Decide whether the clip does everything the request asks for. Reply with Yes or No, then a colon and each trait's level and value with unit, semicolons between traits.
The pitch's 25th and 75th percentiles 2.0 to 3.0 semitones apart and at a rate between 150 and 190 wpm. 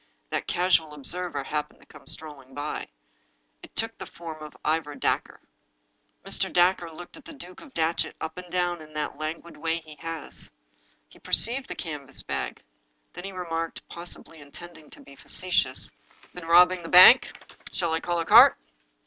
Yes: narrow, 2.6 semitones; average, 165 wpm